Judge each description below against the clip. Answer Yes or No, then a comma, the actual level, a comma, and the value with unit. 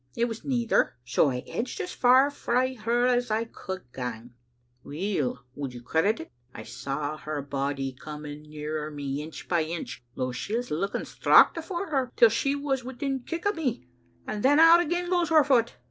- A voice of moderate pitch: No, high, 215 Hz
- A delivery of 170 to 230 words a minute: Yes, average, 190 wpm